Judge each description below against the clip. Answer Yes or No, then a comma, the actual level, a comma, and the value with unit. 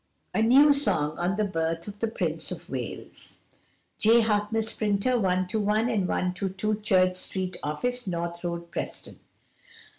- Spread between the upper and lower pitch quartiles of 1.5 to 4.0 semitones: Yes, average, 3.6 semitones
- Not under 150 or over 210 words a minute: No, average, 140 wpm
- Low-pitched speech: No, high, 200 Hz